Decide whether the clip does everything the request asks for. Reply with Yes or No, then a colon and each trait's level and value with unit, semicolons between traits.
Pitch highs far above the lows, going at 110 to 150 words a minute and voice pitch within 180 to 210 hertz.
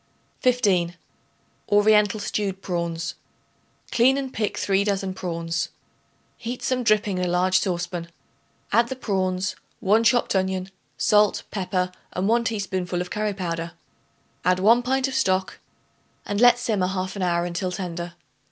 No: average, 3.1 semitones; average, 145 wpm; high, 190 Hz